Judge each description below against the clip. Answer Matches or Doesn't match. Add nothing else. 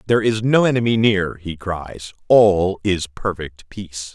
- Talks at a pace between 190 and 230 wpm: Doesn't match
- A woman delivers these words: Doesn't match